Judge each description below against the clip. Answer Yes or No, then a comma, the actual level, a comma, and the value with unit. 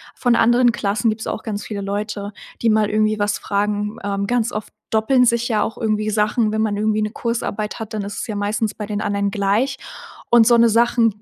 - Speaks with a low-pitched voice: No, high, 215 Hz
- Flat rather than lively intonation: Yes, narrow, 1.8 semitones